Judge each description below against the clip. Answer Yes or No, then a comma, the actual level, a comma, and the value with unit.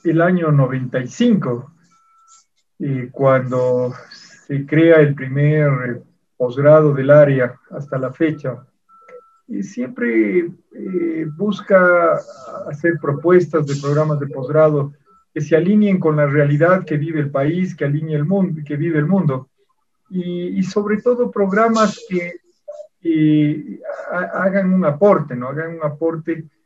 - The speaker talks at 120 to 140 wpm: Yes, average, 130 wpm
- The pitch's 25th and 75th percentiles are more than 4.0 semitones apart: Yes, average, 4.8 semitones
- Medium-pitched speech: Yes, medium, 160 Hz